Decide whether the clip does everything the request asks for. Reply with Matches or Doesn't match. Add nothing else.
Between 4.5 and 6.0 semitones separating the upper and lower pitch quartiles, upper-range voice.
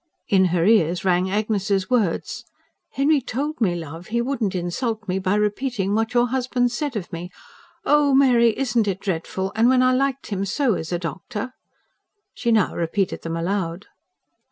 Matches